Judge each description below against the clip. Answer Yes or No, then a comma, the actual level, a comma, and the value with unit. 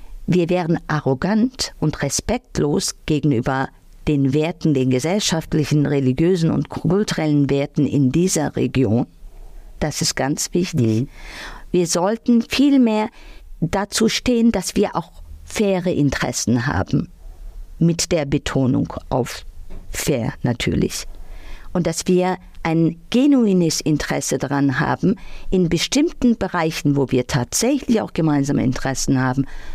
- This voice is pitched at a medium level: Yes, medium, 155 Hz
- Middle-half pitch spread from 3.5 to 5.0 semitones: No, wide, 5.4 semitones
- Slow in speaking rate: Yes, slow, 115 wpm